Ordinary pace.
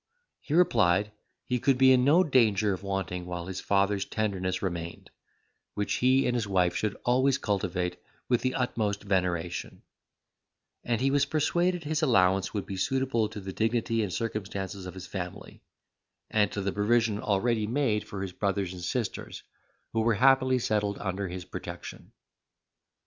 Yes: average, 160 wpm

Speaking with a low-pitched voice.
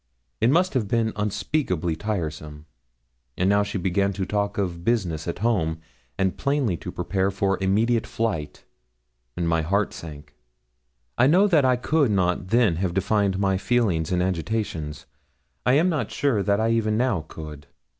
Yes: low, 100 Hz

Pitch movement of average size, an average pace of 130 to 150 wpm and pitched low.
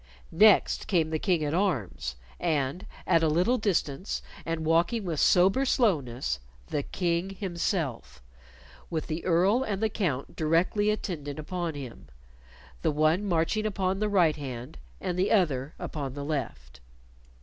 No: average, 5.0 semitones; average, 145 wpm; medium, 165 Hz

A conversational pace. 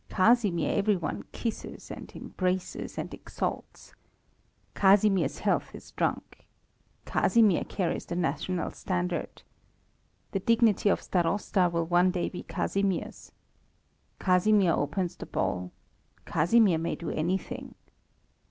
No: slow, 110 wpm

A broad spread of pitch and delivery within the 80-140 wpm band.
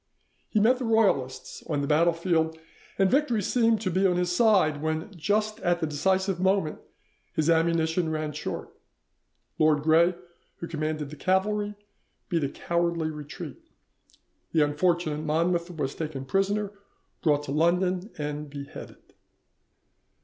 No: average, 3.7 semitones; slow, 135 wpm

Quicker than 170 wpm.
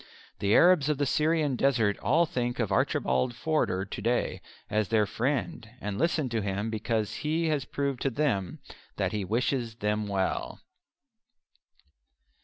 No: average, 150 wpm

